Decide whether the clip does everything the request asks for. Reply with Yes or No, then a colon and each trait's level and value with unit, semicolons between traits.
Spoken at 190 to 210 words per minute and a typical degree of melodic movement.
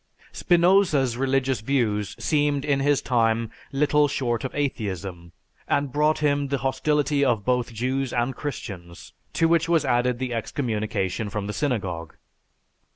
No: average, 140 wpm; average, 4.4 semitones